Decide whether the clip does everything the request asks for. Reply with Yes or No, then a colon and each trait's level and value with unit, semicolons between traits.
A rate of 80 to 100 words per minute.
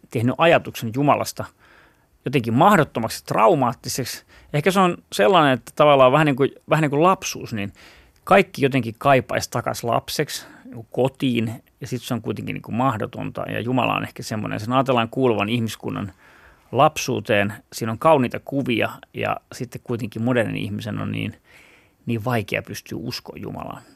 No: fast, 155 wpm